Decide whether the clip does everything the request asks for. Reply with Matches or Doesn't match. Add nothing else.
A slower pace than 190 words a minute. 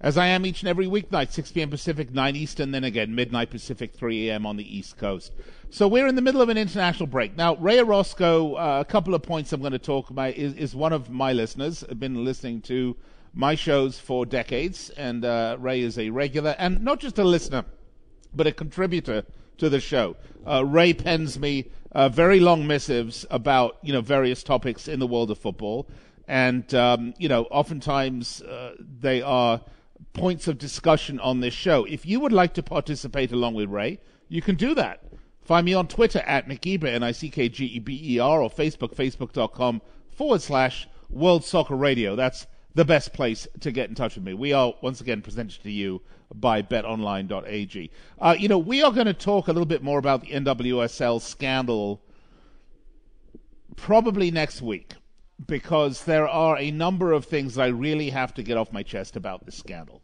Doesn't match